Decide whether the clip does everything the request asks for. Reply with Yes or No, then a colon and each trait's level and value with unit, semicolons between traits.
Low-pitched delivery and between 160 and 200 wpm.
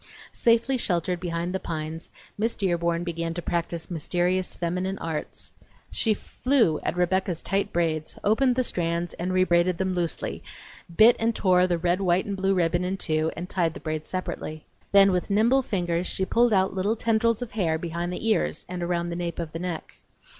No: medium, 180 Hz; average, 185 wpm